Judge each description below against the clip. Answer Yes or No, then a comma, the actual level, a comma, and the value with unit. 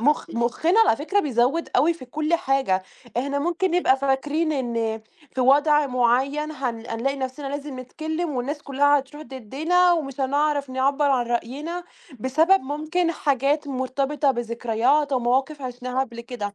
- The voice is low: No, very high, 275 Hz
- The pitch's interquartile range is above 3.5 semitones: No, average, 3.2 semitones